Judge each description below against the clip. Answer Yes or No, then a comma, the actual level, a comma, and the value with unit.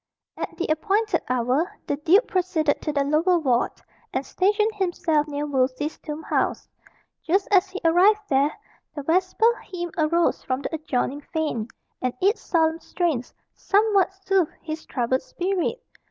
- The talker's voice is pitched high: Yes, very high, 325 Hz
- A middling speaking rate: Yes, average, 150 wpm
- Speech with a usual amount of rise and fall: Yes, average, 4.7 semitones